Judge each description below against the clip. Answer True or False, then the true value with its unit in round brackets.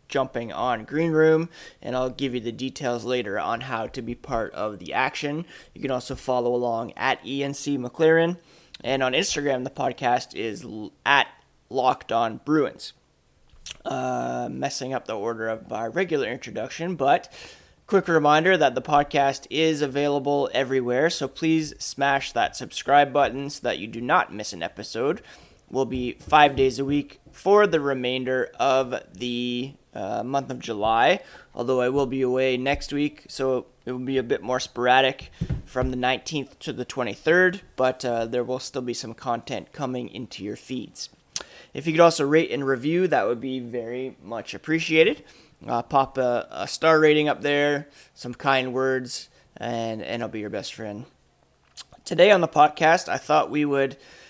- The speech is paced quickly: False (170 wpm)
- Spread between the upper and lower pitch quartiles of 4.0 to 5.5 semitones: False (2.8 semitones)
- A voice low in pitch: True (130 Hz)